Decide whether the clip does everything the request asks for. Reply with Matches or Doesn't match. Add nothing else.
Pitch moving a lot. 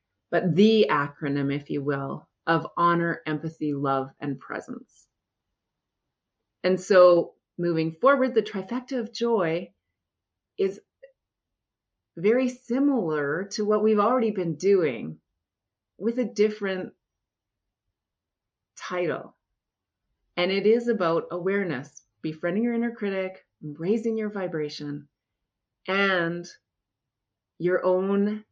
Matches